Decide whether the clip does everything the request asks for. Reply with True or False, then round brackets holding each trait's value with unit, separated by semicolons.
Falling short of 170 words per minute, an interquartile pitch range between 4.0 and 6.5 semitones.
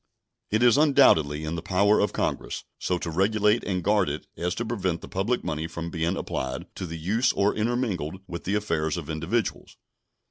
False (190 wpm; 4.6 semitones)